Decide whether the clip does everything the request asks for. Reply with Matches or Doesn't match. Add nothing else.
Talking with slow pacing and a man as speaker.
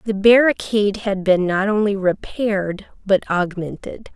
Doesn't match